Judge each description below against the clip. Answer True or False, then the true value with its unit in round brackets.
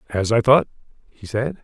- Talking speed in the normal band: True (185 wpm)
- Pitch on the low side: True (120 Hz)